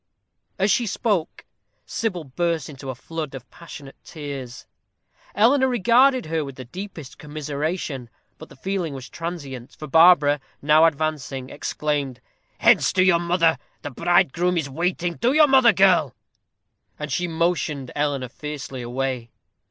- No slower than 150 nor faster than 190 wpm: No, average, 140 wpm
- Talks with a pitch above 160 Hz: No, medium, 155 Hz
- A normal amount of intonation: Yes, average, 4.6 semitones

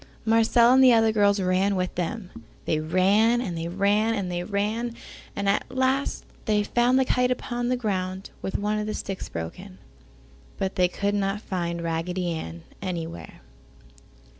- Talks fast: No, average, 165 wpm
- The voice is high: Yes, high, 200 Hz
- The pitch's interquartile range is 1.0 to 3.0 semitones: No, average, 3.9 semitones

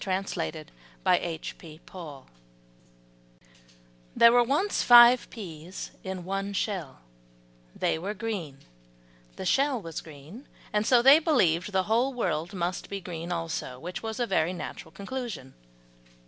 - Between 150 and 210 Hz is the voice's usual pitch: Yes, medium, 185 Hz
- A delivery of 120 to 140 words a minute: Yes, slow, 135 wpm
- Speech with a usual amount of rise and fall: No, wide, 6.1 semitones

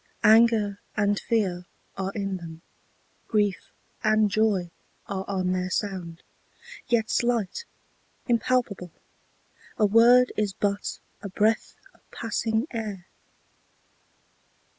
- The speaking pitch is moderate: No, high, 205 Hz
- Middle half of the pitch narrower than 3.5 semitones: Yes, average, 2.9 semitones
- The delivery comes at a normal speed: No, slow, 100 wpm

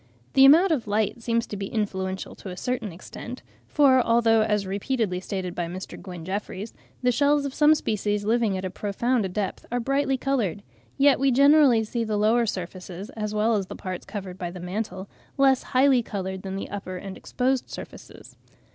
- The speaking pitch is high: Yes, high, 215 Hz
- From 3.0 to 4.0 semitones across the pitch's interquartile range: No, average, 4.9 semitones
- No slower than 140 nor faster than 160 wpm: No, average, 190 wpm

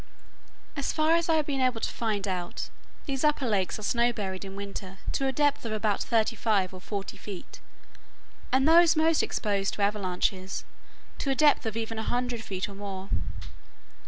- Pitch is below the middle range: No, high, 220 Hz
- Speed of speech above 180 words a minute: Yes, average, 190 wpm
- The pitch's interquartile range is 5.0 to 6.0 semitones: Yes, wide, 5.4 semitones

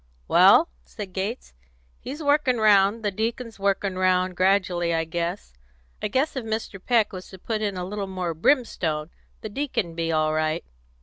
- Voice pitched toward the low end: No, high, 195 Hz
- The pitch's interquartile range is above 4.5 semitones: No, average, 4.2 semitones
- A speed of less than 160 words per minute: No, average, 170 wpm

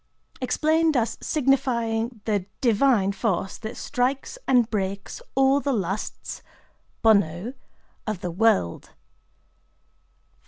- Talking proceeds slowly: Yes, slow, 95 wpm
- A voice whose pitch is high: Yes, high, 225 Hz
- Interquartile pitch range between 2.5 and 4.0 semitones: No, average, 5.0 semitones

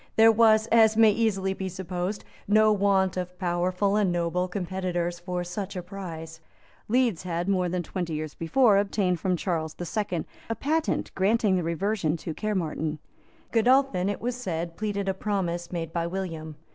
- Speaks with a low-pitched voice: No, medium, 185 Hz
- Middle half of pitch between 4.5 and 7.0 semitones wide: No, average, 3.3 semitones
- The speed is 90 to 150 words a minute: No, average, 170 wpm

